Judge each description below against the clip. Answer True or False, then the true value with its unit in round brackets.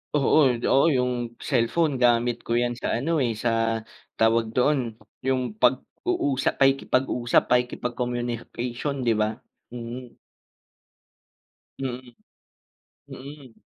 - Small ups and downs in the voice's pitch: True (2.0 semitones)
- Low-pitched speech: True (125 Hz)